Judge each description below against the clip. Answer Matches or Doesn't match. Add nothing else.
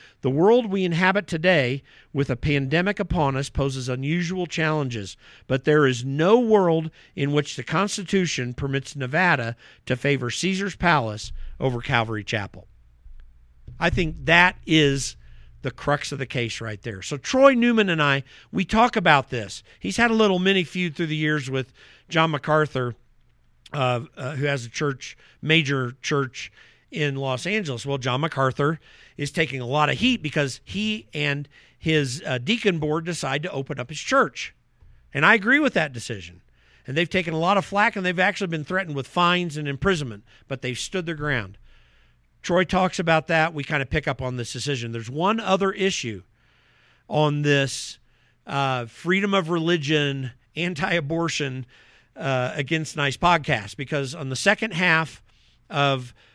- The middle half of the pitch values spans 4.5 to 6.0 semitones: Matches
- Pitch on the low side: Doesn't match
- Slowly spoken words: Doesn't match